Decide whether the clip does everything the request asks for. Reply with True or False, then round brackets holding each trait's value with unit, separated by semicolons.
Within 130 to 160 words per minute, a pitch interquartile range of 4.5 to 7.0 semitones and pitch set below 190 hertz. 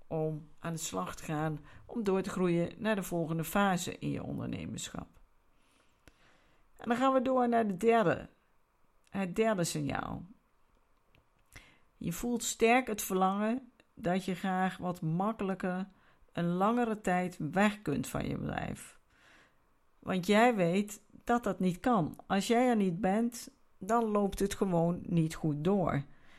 False (150 wpm; 4.8 semitones; 195 Hz)